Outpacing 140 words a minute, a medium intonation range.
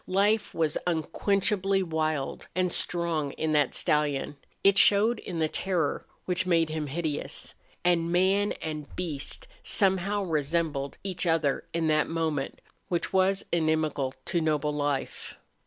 No: slow, 135 wpm; average, 3.7 semitones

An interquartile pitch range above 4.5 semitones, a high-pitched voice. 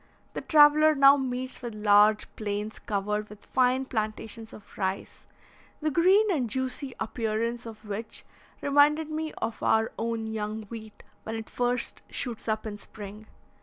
No: average, 3.8 semitones; high, 225 Hz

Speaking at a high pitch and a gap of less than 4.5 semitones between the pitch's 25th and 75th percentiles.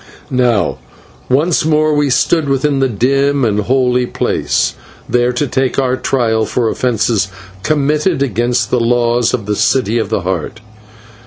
No: low, 125 Hz; average, 3.3 semitones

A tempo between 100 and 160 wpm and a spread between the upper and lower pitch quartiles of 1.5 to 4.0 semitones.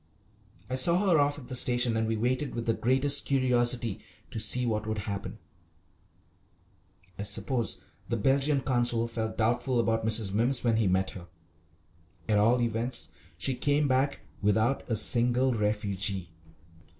Yes: average, 150 wpm; average, 3.0 semitones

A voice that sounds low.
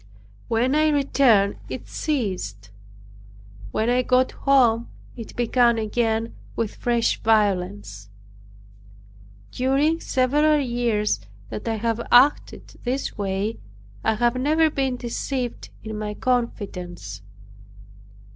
No: high, 235 Hz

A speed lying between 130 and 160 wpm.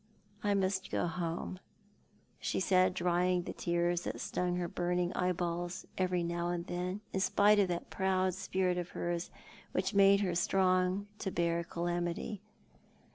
Yes: average, 155 wpm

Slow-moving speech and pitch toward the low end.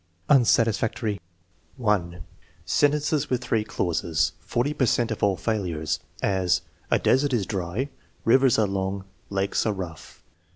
Yes: slow, 130 wpm; low, 105 Hz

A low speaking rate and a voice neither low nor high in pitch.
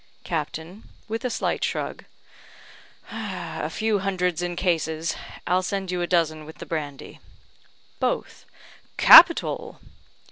Yes: slow, 115 wpm; medium, 175 Hz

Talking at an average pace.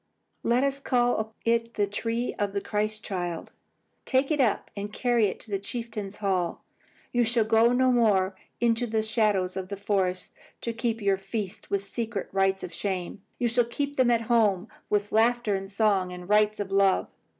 Yes: average, 185 wpm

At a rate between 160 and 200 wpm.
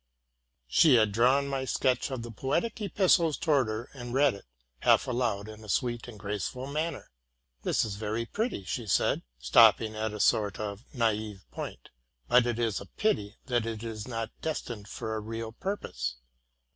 Yes: average, 185 wpm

